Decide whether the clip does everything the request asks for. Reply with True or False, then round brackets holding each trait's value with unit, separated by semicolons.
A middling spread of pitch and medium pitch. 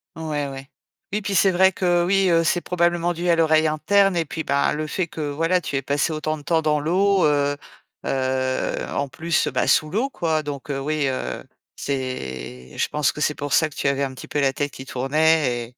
True (3.7 semitones; 155 Hz)